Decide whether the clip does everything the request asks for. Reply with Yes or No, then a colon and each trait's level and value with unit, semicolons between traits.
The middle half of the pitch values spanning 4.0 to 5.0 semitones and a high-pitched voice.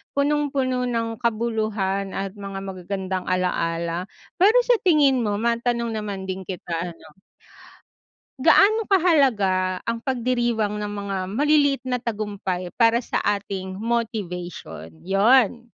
Yes: average, 4.7 semitones; high, 220 Hz